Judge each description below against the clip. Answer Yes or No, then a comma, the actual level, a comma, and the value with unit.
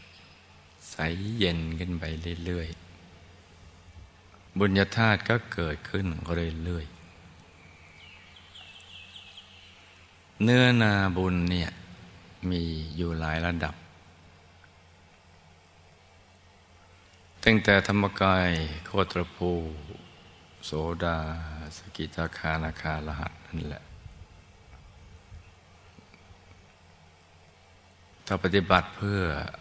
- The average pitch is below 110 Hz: Yes, very low, 90 Hz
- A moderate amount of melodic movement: No, narrow, 2.0 semitones